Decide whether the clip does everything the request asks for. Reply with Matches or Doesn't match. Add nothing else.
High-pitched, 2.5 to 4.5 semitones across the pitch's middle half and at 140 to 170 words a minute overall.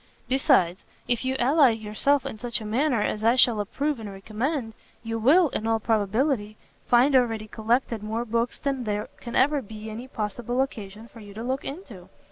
Doesn't match